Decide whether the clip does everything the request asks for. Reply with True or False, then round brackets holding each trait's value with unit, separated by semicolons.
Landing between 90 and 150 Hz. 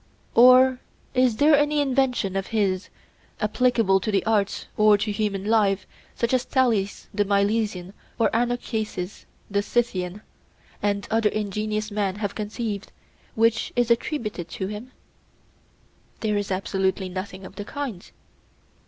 False (210 Hz)